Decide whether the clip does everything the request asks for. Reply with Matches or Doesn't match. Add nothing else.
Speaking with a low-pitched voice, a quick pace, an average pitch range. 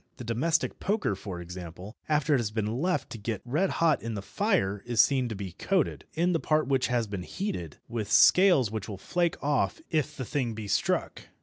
Doesn't match